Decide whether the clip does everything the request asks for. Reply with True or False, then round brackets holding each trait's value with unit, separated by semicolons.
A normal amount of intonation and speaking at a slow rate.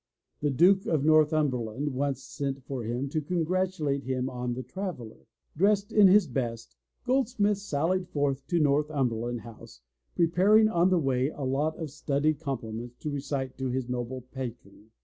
False (4.9 semitones; 160 wpm)